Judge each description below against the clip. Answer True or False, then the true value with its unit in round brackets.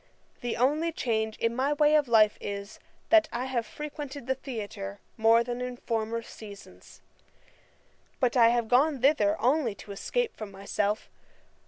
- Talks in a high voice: True (240 Hz)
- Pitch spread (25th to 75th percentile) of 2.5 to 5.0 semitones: True (4.4 semitones)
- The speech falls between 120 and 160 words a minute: True (155 wpm)